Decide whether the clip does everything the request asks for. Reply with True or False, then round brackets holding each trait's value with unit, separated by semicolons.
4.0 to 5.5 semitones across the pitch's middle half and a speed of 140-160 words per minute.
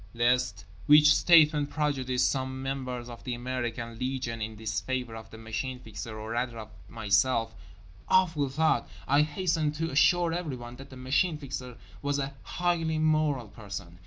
True (4.7 semitones; 145 wpm)